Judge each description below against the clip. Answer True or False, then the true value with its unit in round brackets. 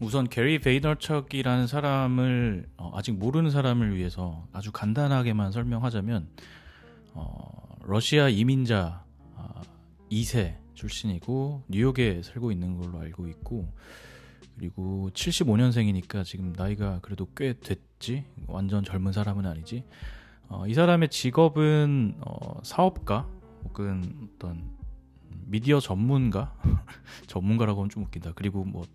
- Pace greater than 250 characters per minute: True (270 characters per minute)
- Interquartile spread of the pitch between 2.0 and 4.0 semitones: False (5.6 semitones)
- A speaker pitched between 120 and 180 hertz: False (105 Hz)